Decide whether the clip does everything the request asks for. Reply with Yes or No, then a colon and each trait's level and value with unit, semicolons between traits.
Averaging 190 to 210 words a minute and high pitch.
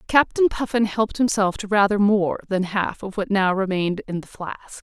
Yes: average, 200 wpm; high, 205 Hz